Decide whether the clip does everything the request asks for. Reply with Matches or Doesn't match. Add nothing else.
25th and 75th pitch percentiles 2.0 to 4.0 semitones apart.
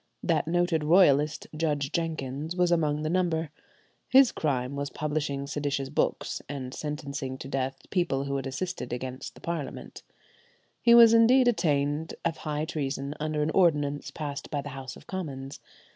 Matches